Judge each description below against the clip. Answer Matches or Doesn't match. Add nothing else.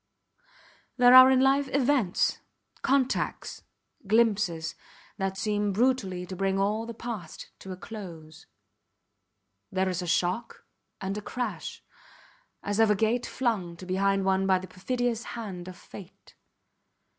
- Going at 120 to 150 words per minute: Matches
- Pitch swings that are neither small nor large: Matches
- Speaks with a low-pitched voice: Doesn't match